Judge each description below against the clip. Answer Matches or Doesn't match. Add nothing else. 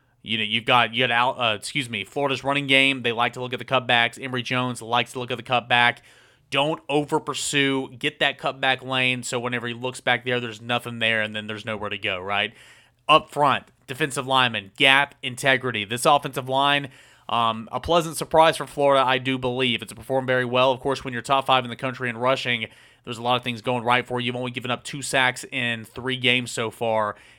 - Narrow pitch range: Matches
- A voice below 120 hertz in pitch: Doesn't match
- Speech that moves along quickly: Matches